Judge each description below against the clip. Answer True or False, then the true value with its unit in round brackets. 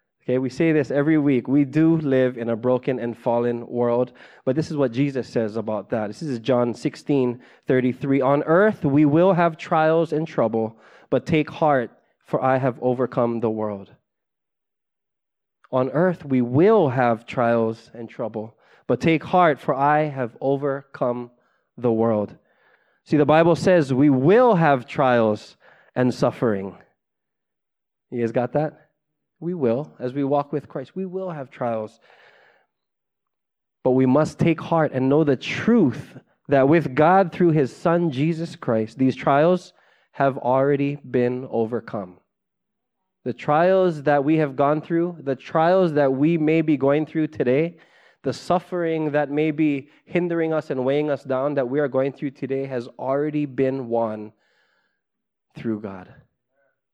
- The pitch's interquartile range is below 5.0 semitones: True (4.1 semitones)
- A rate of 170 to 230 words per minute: False (155 wpm)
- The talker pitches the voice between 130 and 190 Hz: True (140 Hz)